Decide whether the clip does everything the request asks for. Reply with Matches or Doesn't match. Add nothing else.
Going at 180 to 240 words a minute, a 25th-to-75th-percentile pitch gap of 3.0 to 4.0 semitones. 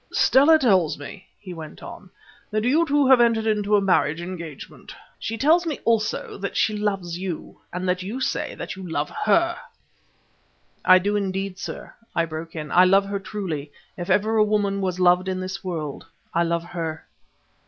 Matches